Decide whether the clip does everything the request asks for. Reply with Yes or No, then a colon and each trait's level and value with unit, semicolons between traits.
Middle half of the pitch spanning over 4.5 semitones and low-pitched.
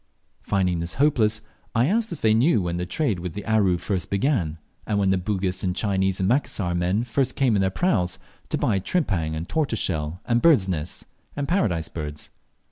Yes: average, 5.3 semitones; very low, 95 Hz